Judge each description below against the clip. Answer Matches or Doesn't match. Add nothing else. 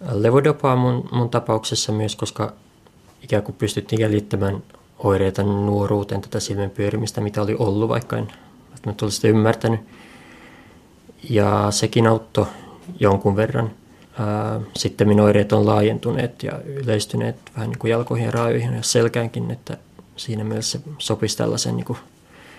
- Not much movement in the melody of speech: Matches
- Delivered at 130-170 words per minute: Matches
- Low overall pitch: Matches